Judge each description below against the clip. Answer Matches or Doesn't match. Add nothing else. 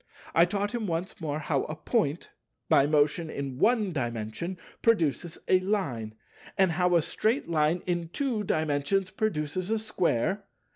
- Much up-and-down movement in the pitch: Doesn't match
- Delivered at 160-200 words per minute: Doesn't match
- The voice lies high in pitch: Doesn't match